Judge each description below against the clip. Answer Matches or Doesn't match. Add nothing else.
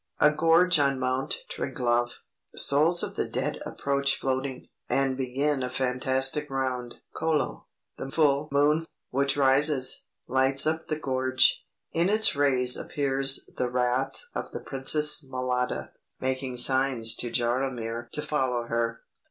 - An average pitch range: Doesn't match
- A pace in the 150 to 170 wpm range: Doesn't match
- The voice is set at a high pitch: Doesn't match